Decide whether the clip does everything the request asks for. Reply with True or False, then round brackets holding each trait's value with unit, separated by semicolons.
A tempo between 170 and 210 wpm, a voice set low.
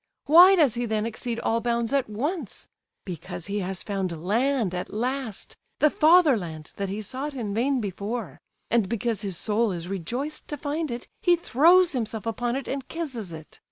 False (180 wpm; 235 Hz)